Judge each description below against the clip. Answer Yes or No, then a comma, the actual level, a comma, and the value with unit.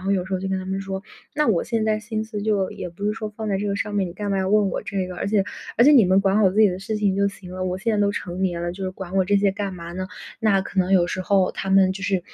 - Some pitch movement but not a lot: No, narrow, 1.9 semitones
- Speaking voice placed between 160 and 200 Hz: Yes, high, 195 Hz